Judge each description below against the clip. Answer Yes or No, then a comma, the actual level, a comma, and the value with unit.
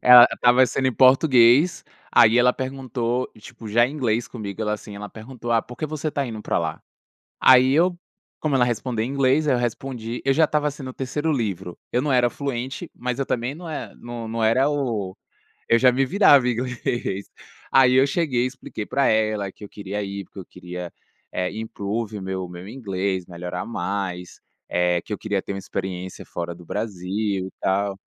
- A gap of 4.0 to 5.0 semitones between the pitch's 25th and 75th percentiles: Yes, average, 4.7 semitones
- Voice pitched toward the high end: No, low, 120 Hz